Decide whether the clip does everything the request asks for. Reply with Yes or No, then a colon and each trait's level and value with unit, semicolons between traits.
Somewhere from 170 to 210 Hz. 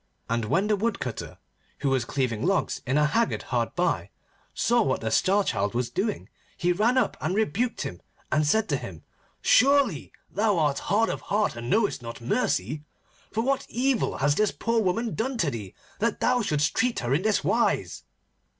Yes: high, 190 Hz